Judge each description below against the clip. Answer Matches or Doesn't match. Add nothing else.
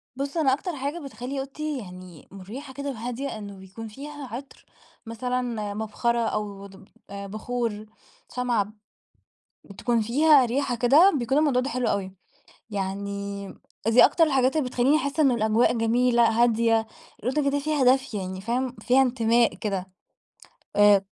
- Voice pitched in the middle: Doesn't match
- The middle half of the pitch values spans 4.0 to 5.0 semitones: Matches